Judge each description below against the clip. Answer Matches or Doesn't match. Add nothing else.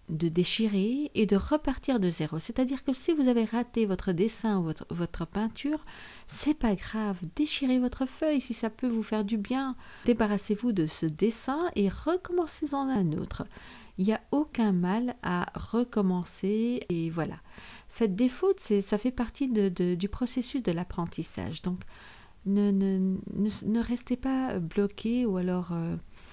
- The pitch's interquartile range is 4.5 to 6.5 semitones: Matches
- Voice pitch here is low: Doesn't match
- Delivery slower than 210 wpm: Matches